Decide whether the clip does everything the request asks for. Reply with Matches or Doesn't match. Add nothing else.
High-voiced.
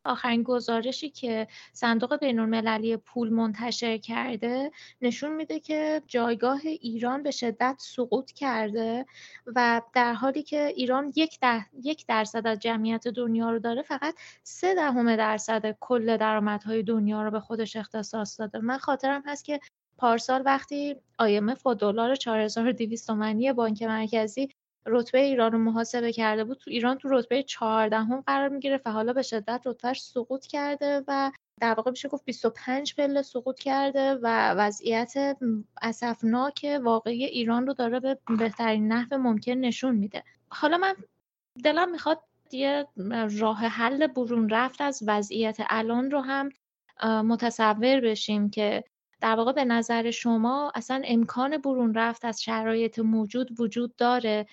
Matches